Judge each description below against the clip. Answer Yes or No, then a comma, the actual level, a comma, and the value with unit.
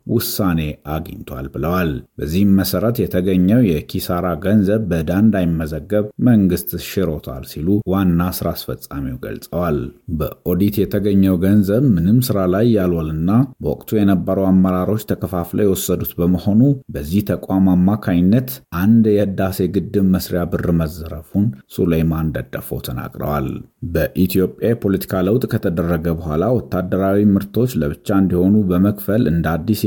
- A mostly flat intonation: No, average, 3.1 semitones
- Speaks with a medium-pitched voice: No, very low, 95 Hz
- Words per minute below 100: No, fast, 110 wpm